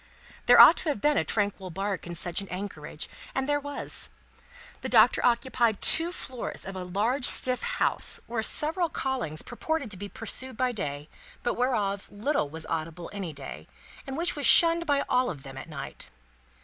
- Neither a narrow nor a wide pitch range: No, wide, 7.1 semitones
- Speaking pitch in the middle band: No, high, 220 Hz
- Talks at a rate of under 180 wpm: No, average, 185 wpm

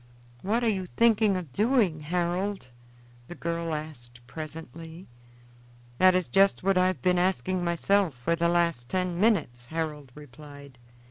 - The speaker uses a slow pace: No, average, 145 wpm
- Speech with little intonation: No, average, 3.7 semitones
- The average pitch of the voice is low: No, medium, 170 Hz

